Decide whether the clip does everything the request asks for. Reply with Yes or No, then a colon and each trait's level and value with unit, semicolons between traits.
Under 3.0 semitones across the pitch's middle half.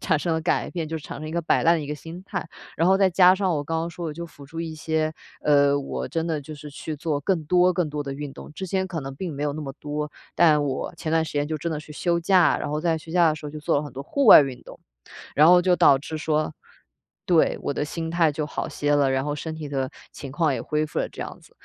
Yes: narrow, 2.5 semitones